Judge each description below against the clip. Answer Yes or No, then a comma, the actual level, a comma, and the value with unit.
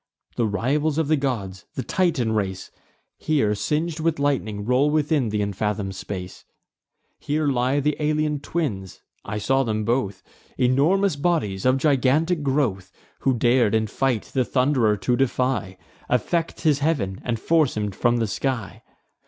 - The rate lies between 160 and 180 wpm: No, average, 150 wpm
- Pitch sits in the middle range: No, low, 130 Hz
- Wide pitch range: Yes, wide, 5.9 semitones